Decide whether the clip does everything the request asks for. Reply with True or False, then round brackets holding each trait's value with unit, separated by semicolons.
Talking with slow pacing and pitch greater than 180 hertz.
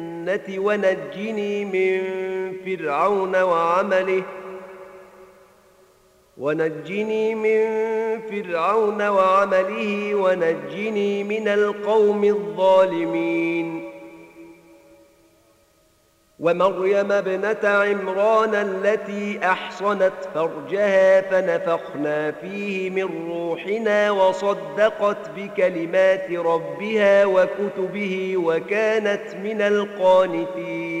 True (55 wpm; 190 Hz)